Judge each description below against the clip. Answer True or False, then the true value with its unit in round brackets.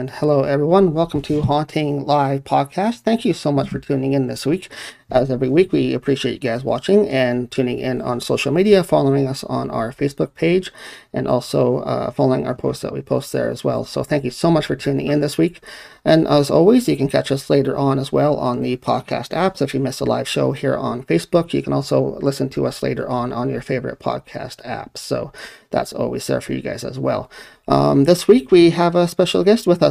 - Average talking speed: False (230 wpm)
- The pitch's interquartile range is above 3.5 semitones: True (4.6 semitones)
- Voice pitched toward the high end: False (140 Hz)